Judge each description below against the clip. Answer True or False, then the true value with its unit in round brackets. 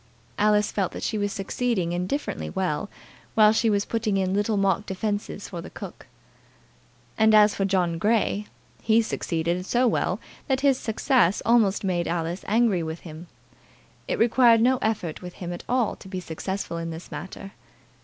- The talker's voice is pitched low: False (200 Hz)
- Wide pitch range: False (3.8 semitones)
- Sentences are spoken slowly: False (170 wpm)